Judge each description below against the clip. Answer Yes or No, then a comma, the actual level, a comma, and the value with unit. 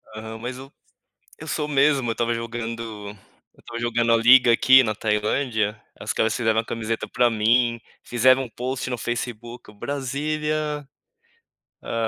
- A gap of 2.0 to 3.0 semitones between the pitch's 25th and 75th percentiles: Yes, narrow, 2.6 semitones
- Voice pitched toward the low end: Yes, low, 120 Hz